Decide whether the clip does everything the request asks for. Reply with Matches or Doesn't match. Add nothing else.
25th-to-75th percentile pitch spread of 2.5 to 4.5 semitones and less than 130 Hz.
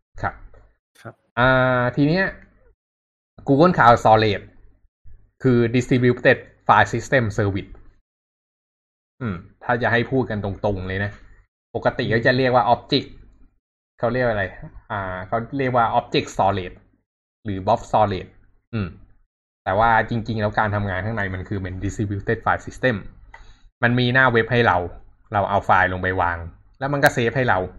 Matches